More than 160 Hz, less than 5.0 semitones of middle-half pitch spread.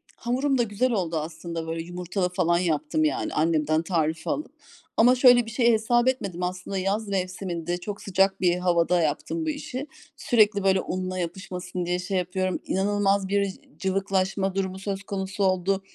Yes: high, 190 Hz; narrow, 2.5 semitones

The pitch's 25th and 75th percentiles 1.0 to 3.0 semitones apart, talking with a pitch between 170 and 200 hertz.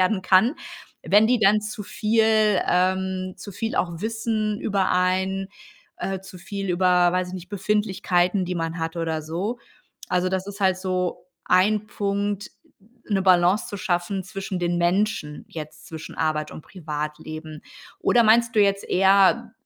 Yes: average, 2.7 semitones; high, 190 Hz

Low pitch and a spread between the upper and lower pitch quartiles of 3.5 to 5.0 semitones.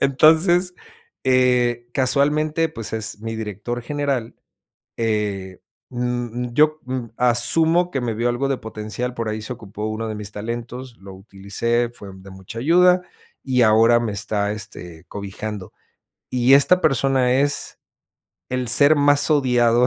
Yes: low, 120 Hz; average, 4.1 semitones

